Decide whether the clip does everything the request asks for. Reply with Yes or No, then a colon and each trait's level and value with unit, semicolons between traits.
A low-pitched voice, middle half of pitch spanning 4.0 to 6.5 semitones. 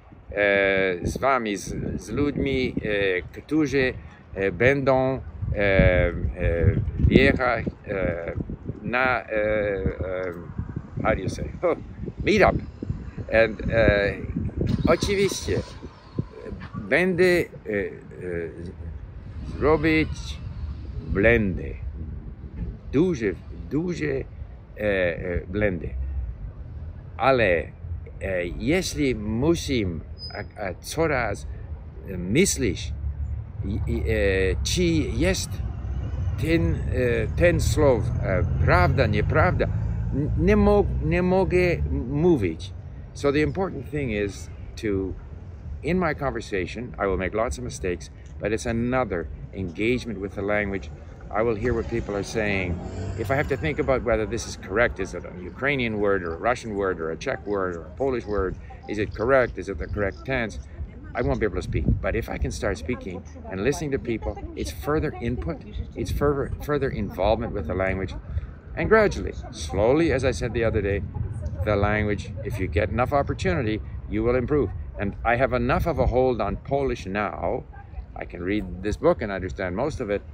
Yes: low, 100 Hz; average, 5.2 semitones